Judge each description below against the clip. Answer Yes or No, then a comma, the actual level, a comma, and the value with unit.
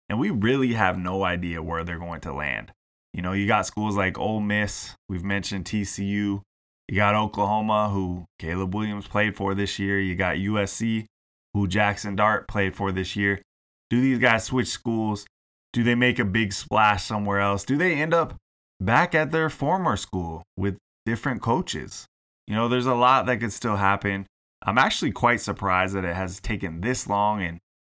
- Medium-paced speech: Yes, average, 190 wpm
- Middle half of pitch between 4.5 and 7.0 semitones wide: No, average, 2.8 semitones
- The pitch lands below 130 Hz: Yes, low, 100 Hz